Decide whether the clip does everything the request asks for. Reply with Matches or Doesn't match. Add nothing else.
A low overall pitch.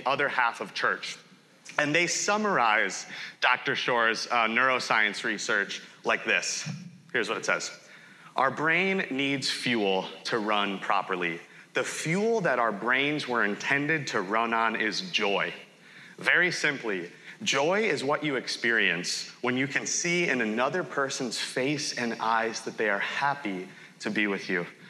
Matches